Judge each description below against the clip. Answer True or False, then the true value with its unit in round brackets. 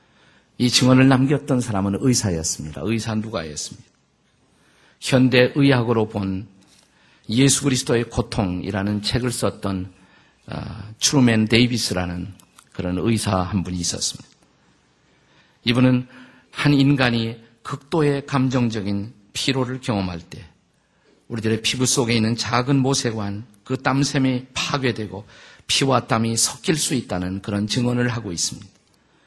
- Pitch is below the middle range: True (115 Hz)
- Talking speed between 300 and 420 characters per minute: False (275 characters per minute)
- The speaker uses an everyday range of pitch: True (4.3 semitones)